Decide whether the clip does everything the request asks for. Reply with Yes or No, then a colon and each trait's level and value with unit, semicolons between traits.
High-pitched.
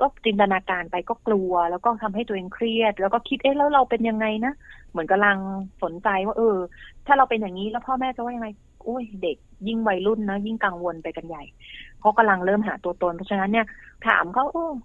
Yes: high, 215 Hz